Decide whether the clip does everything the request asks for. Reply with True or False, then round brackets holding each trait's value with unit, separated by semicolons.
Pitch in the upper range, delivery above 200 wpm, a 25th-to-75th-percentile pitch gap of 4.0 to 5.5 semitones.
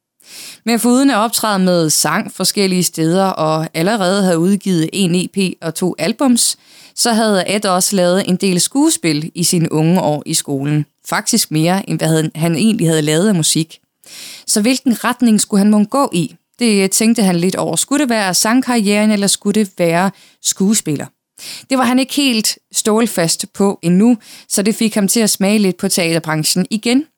False (195 Hz; 180 wpm; 4.7 semitones)